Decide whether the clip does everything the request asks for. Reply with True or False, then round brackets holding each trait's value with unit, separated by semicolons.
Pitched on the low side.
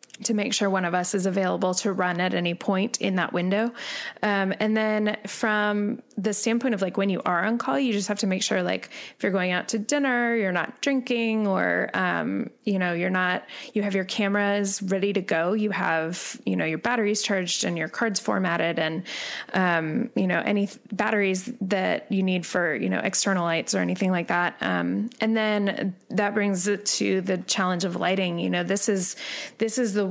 False (200 Hz)